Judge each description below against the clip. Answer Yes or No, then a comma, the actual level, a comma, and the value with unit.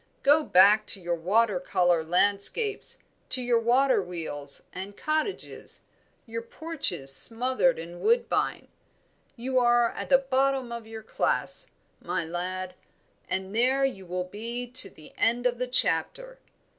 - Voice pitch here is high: Yes, high, 230 Hz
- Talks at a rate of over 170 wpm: No, average, 140 wpm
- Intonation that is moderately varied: No, wide, 6.0 semitones